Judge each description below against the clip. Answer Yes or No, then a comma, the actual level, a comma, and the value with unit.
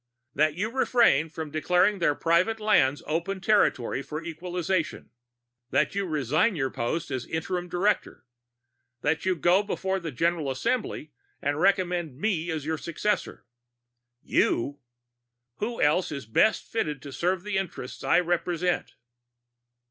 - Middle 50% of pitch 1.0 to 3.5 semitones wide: No, average, 4.1 semitones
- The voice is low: No, medium, 170 Hz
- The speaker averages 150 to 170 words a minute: No, slow, 135 wpm